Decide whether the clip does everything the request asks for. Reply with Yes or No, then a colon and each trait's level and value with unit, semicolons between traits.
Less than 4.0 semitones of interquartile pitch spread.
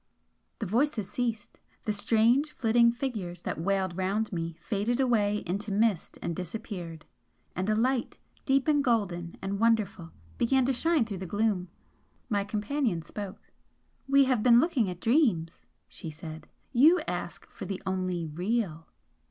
No: average, 4.8 semitones